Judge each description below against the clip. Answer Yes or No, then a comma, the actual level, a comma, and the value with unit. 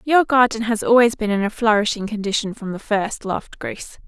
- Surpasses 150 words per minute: Yes, fast, 205 wpm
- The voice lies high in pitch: Yes, high, 220 Hz